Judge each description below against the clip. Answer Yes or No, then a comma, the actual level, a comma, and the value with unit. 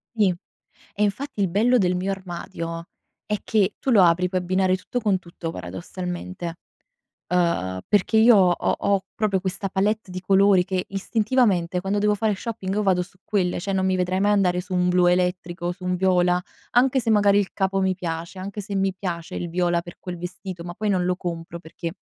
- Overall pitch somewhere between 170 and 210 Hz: Yes, medium, 185 Hz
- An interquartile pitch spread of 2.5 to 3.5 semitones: No, narrow, 2.1 semitones